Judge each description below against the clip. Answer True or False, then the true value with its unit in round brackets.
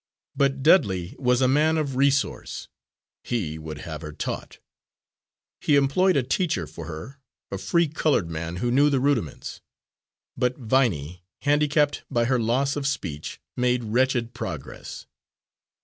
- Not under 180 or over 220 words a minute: False (140 wpm)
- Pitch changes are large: True (7.2 semitones)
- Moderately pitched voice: False (125 Hz)